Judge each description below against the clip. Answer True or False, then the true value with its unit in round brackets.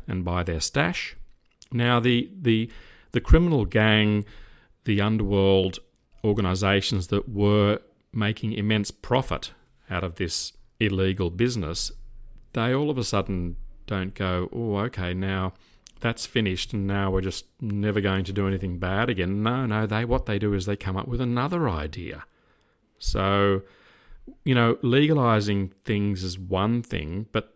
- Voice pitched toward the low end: True (100 Hz)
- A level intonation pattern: False (3.4 semitones)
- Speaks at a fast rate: False (150 wpm)